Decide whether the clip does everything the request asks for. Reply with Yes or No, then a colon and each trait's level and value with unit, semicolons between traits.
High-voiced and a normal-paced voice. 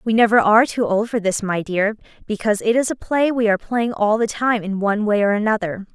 No: high, 215 Hz; fast, 250 wpm